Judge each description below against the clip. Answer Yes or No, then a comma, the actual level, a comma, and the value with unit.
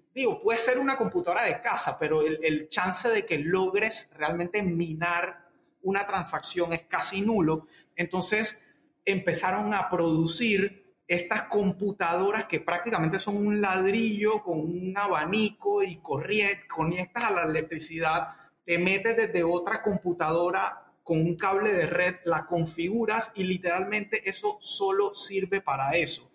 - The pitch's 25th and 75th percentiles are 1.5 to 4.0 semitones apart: Yes, average, 3.7 semitones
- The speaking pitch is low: No, medium, 185 Hz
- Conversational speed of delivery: Yes, average, 135 wpm